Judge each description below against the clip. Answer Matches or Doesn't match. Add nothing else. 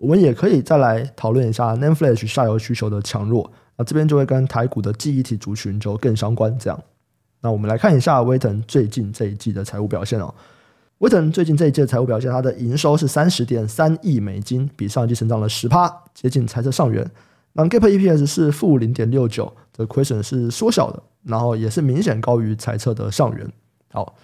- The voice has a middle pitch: Doesn't match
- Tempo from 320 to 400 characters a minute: Matches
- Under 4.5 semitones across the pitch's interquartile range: Doesn't match